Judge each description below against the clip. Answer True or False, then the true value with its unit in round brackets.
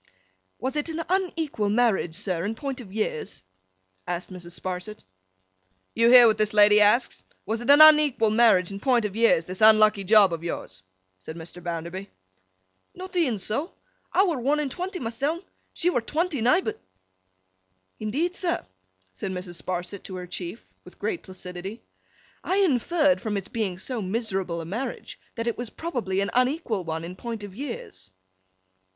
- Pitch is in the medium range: False (220 Hz)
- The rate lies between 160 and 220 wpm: True (165 wpm)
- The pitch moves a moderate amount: False (6.6 semitones)